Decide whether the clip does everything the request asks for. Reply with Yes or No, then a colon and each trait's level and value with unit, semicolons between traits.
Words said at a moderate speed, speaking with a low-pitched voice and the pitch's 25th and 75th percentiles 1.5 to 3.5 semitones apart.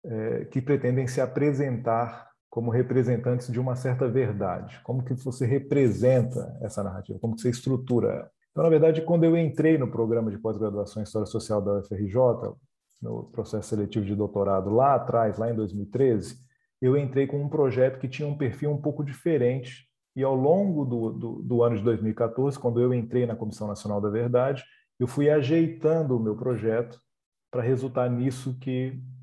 Yes: average, 175 wpm; low, 125 Hz; average, 3.0 semitones